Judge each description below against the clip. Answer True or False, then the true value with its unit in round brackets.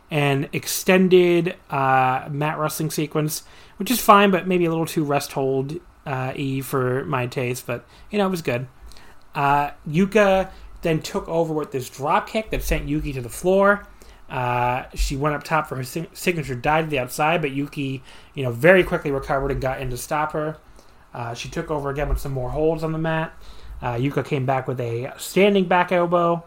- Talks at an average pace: True (195 wpm)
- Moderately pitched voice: True (150 Hz)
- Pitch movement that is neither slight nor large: True (4.2 semitones)